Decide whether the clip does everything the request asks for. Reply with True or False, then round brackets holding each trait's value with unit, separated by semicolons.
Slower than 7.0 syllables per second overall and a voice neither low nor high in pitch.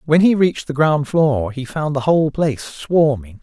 True (4.9 syllables/s; 145 Hz)